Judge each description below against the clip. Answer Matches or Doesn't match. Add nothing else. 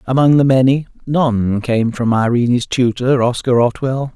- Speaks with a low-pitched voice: Matches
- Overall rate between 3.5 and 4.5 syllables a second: Matches